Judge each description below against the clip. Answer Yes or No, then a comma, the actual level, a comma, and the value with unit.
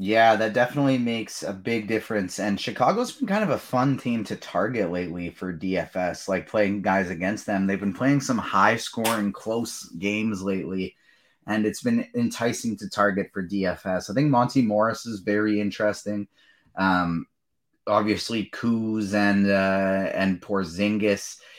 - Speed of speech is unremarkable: Yes, average, 155 wpm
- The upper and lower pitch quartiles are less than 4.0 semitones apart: Yes, average, 3.0 semitones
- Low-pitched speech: Yes, low, 105 Hz